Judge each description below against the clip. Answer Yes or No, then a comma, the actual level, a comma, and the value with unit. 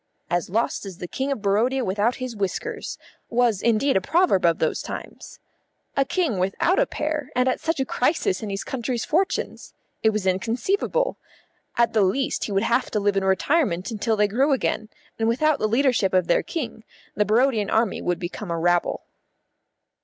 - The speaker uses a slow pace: No, average, 185 wpm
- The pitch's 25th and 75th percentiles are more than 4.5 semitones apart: Yes, average, 5.3 semitones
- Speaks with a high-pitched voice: Yes, high, 225 Hz